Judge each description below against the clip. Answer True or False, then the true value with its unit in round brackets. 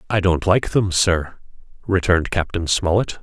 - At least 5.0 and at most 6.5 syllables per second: False (4.7 syllables/s)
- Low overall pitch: True (90 Hz)